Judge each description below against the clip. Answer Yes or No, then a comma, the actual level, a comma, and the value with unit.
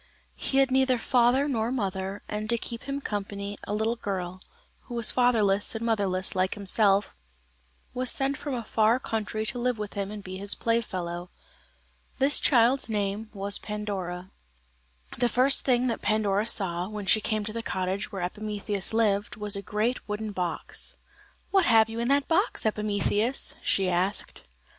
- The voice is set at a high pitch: Yes, high, 215 Hz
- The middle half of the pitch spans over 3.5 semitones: No, average, 3.1 semitones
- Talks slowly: No, average, 165 wpm